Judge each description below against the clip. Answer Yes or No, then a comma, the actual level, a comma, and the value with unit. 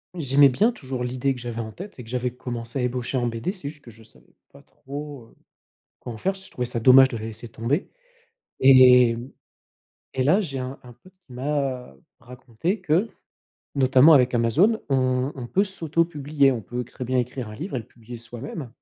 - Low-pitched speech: Yes, low, 130 Hz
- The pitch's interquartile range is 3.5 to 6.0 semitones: No, average, 3.1 semitones